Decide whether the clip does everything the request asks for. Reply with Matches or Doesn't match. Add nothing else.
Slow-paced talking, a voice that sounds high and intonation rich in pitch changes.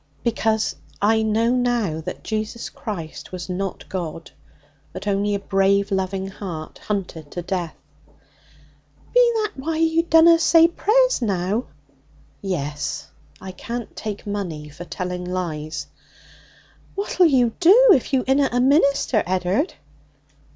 Matches